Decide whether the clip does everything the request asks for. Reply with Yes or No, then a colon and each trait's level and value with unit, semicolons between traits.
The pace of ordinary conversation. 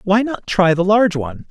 No: fast, 240 wpm